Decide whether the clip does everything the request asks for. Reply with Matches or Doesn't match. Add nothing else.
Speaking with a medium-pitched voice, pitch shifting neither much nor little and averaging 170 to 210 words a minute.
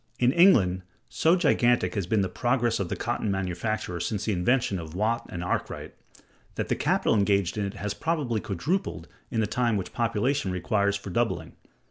Doesn't match